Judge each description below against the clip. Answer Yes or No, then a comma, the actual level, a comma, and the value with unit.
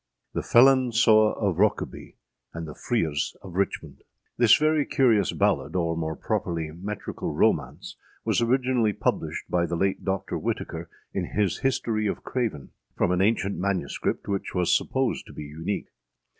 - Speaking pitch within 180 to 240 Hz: No, low, 100 Hz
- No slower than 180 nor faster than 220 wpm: No, average, 155 wpm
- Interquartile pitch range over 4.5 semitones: Yes, wide, 5.4 semitones